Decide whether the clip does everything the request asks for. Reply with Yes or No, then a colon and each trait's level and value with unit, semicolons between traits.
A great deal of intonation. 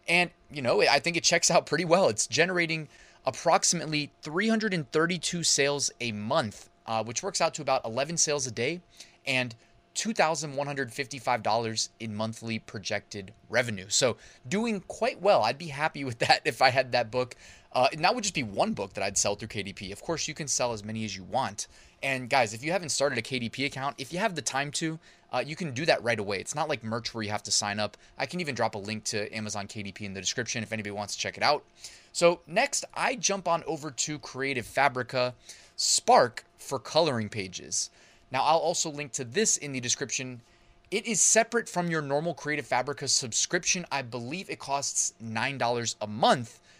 Yes: wide, 6.3 semitones